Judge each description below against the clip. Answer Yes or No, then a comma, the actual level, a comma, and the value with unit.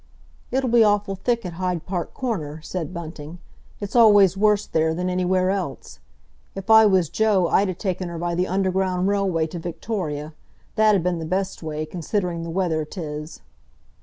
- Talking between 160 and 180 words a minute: Yes, average, 170 wpm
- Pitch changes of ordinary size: Yes, average, 3.2 semitones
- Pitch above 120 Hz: Yes, medium, 185 Hz